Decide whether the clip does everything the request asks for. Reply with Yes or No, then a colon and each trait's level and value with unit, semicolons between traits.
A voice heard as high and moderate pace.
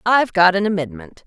No: medium, 180 Hz; average, 190 wpm